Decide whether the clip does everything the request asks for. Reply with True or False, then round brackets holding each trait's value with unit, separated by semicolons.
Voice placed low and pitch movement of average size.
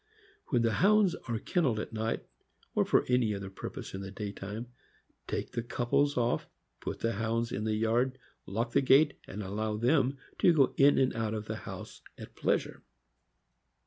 True (115 Hz; 3.3 semitones)